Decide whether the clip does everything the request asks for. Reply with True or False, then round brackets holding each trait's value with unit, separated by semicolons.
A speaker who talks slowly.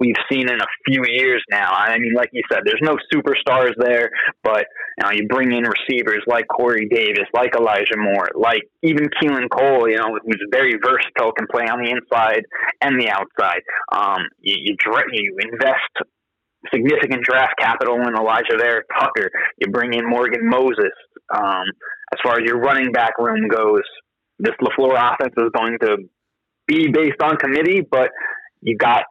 False (175 wpm)